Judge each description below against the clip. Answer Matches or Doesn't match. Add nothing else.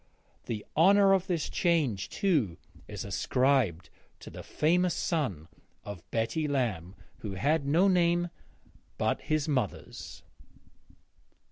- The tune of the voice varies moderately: Doesn't match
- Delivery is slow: Matches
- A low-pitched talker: Doesn't match